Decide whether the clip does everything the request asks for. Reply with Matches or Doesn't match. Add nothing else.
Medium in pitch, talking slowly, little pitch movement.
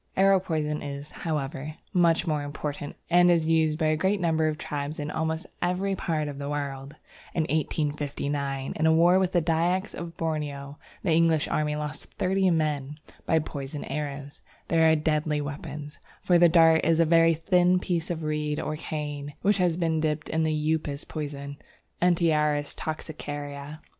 Doesn't match